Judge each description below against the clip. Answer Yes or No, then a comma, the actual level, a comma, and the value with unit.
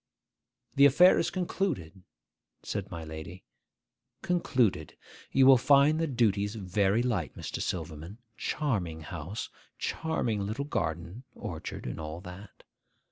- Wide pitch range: Yes, wide, 8.3 semitones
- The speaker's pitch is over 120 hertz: No, low, 105 Hz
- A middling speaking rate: No, slow, 120 wpm